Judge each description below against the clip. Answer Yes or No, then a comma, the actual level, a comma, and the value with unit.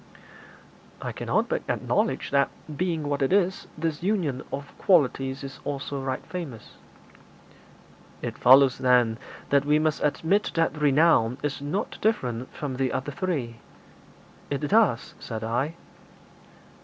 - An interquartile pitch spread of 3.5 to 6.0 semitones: Yes, average, 3.9 semitones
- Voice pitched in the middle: Yes, medium, 145 Hz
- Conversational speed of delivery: No, slow, 130 wpm